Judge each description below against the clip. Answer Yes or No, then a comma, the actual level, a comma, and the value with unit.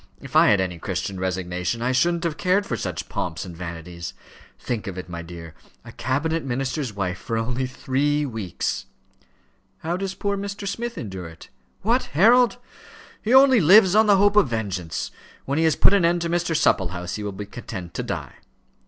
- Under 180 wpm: No, average, 190 wpm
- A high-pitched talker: No, low, 130 Hz